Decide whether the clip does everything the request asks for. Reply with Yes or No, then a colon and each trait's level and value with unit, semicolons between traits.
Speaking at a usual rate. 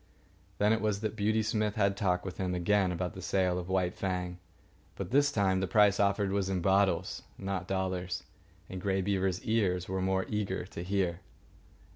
Yes: average, 185 wpm